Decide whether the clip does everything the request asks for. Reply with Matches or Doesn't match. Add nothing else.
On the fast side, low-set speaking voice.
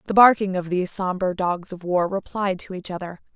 Doesn't match